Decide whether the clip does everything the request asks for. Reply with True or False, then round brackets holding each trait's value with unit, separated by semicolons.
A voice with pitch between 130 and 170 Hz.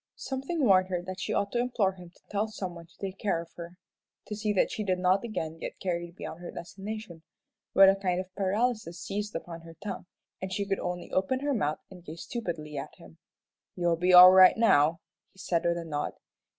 False (185 Hz)